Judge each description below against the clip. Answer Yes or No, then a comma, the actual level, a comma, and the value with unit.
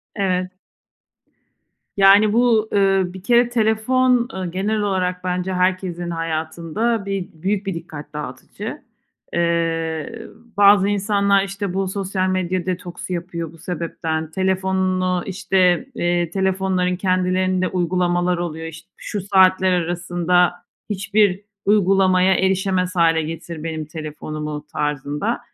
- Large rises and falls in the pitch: No, narrow, 2.4 semitones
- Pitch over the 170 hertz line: Yes, medium, 185 Hz